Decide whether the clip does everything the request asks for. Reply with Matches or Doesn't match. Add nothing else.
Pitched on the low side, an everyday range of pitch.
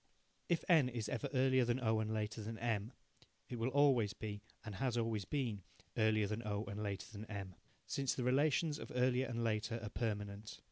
Matches